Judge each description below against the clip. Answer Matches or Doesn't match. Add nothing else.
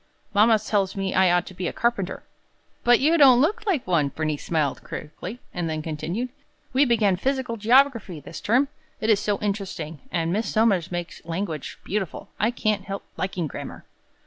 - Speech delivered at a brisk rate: Doesn't match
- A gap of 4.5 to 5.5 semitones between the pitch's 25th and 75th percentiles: Matches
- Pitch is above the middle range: Matches